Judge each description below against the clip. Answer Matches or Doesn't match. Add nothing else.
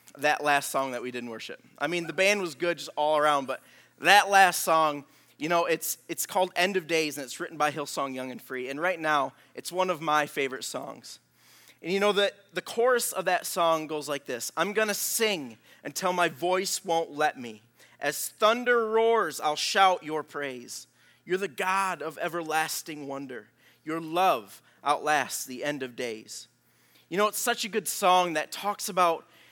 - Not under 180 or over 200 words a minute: Matches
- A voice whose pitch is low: Doesn't match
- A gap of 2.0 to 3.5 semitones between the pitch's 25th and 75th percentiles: Doesn't match